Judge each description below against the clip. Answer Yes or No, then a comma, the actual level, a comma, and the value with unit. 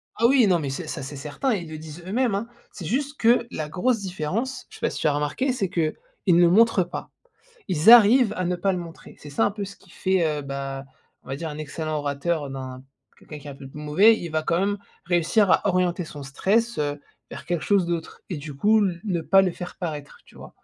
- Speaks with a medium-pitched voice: Yes, medium, 175 Hz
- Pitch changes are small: No, average, 5.2 semitones